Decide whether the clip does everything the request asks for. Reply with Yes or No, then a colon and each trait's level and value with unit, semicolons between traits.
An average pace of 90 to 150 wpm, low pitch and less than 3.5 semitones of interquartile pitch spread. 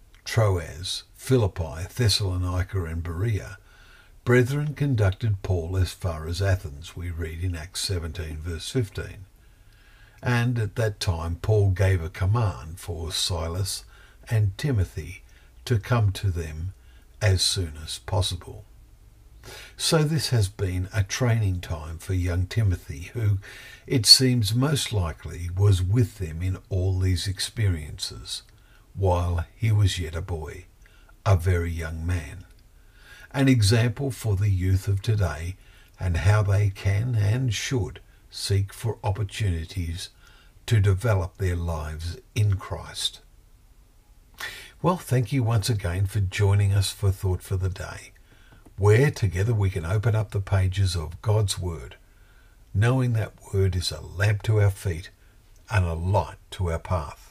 Yes: average, 140 wpm; very low, 95 Hz; average, 2.9 semitones